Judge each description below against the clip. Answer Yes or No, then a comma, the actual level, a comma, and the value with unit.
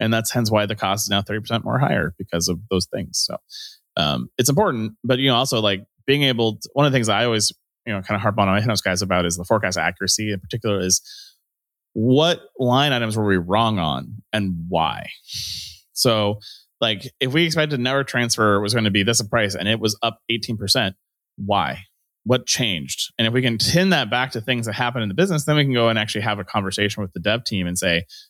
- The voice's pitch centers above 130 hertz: No, low, 110 Hz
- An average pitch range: Yes, average, 3.5 semitones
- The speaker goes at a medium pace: No, fast, 230 wpm